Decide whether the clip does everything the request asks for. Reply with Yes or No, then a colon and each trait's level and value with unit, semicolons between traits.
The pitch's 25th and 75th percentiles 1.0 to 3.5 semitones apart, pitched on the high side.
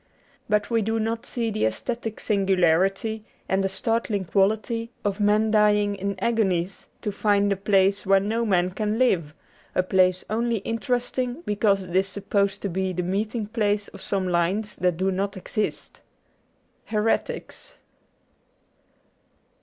Yes: narrow, 2.5 semitones; high, 205 Hz